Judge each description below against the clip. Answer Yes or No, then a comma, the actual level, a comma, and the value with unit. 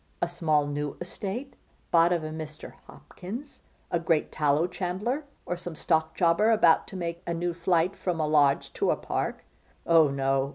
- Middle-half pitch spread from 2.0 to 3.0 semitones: Yes, narrow, 2.5 semitones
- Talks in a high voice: No, medium, 170 Hz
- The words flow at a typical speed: Yes, average, 175 wpm